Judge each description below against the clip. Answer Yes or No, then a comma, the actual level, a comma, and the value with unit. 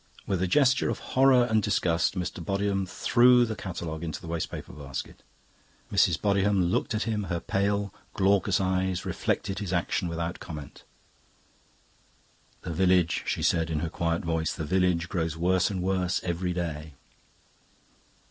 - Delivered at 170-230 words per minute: No, average, 155 wpm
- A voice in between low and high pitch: No, very low, 90 Hz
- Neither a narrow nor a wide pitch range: Yes, average, 3.0 semitones